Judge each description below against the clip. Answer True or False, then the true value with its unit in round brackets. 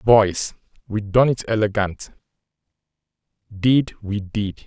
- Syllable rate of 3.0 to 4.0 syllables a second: True (3.3 syllables/s)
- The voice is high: False (105 Hz)